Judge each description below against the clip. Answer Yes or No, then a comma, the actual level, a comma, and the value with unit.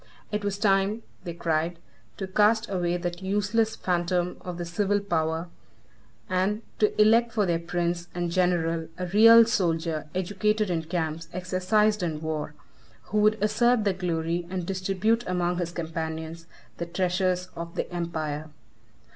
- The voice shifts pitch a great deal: No, average, 3.3 semitones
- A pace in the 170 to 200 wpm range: No, average, 145 wpm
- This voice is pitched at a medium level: Yes, medium, 180 Hz